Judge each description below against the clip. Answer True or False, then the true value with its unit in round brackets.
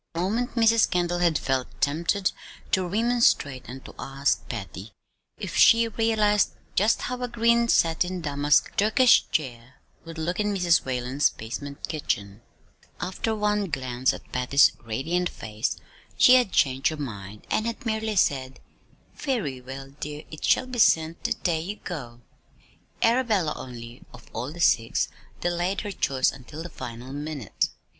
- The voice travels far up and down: True (8.0 semitones)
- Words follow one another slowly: False (155 wpm)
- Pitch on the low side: False (160 Hz)